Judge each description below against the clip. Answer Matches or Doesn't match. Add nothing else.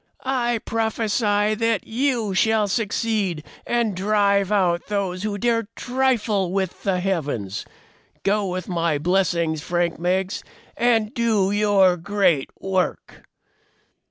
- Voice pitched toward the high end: Matches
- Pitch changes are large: Doesn't match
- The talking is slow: Matches